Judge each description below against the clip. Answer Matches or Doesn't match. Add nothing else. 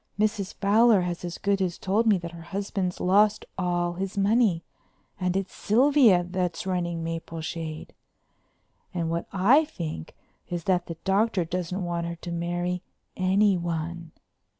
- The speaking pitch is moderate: Matches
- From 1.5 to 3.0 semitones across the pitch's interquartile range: Matches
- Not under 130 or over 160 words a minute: Matches